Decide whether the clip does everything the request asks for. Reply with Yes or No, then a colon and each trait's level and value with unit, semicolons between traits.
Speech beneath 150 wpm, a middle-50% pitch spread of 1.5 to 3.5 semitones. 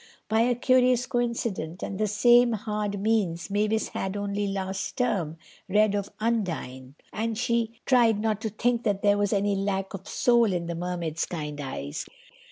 No: average, 170 wpm; average, 3.2 semitones